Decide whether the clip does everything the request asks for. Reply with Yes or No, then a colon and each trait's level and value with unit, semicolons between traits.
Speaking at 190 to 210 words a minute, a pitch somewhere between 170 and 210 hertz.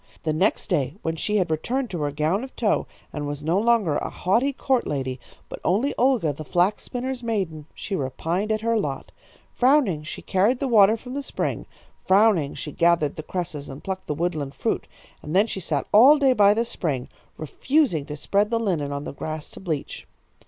Yes: average, 200 wpm; medium, 185 Hz